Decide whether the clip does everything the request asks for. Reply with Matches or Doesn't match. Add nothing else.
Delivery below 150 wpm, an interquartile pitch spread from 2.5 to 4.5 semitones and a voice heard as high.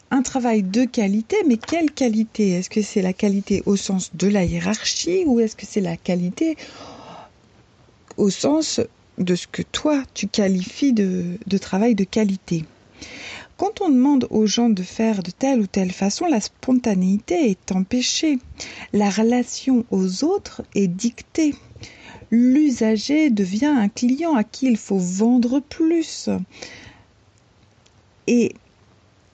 Doesn't match